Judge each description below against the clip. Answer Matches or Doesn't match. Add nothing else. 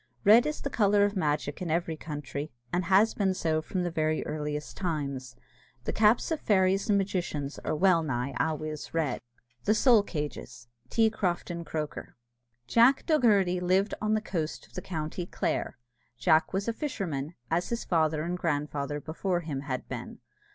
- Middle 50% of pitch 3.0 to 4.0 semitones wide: Doesn't match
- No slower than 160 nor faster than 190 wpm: Matches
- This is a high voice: Doesn't match